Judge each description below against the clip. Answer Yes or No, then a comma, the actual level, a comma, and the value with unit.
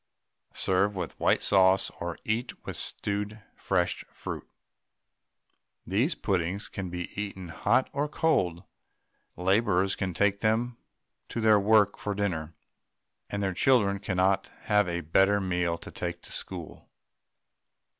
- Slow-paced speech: Yes, slow, 130 wpm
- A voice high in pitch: No, low, 100 Hz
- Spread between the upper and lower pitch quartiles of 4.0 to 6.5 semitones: No, narrow, 2.6 semitones